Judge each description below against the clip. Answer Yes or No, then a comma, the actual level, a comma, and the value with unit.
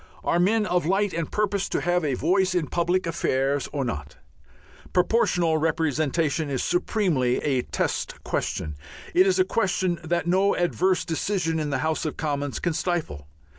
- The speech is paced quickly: No, average, 165 wpm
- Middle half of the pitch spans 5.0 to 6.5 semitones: No, average, 4.0 semitones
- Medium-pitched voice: Yes, medium, 170 Hz